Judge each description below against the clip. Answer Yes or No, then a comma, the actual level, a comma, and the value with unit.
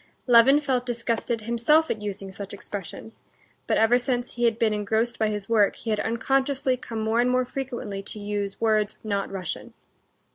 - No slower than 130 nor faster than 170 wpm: No, average, 180 wpm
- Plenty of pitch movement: No, average, 2.9 semitones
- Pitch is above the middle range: Yes, high, 225 Hz